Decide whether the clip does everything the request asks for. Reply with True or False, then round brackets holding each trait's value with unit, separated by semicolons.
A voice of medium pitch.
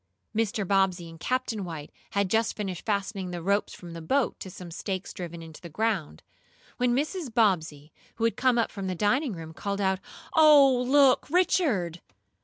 False (200 Hz)